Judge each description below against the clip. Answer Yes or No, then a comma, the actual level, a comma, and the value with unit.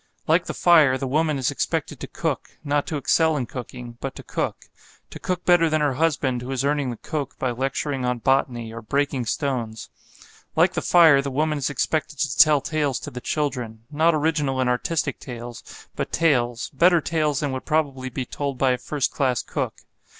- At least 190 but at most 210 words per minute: Yes, average, 200 wpm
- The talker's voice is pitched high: No, medium, 140 Hz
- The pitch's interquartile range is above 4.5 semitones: No, average, 3.4 semitones